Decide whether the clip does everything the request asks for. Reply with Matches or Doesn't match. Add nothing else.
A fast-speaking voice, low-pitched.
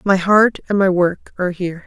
Doesn't match